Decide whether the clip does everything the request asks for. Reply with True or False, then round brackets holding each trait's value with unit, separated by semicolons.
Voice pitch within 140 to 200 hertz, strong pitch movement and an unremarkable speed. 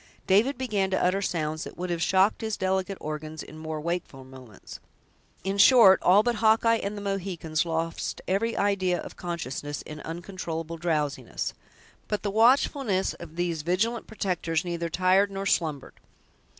False (185 Hz; 3.7 semitones; 155 wpm)